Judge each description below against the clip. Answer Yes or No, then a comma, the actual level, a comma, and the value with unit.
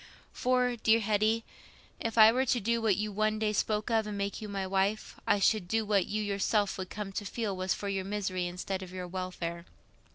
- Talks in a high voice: Yes, high, 205 Hz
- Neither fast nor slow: No, fast, 220 wpm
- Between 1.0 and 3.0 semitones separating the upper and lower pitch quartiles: Yes, narrow, 2.4 semitones